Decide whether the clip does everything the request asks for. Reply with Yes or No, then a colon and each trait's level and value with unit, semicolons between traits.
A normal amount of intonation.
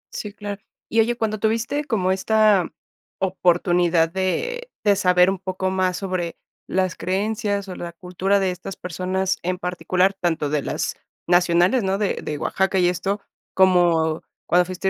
No: narrow, 2.2 semitones